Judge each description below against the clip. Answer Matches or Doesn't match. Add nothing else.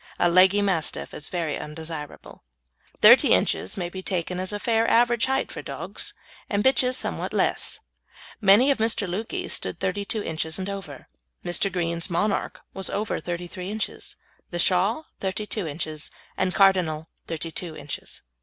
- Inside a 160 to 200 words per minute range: Doesn't match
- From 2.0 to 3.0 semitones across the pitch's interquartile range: Doesn't match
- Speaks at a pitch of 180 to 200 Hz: Matches